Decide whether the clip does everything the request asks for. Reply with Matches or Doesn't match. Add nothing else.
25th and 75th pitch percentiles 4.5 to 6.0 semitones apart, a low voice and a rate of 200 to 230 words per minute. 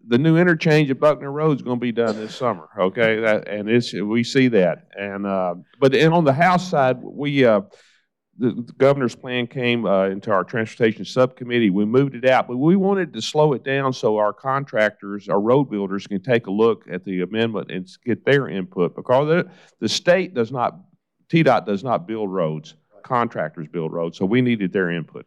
Matches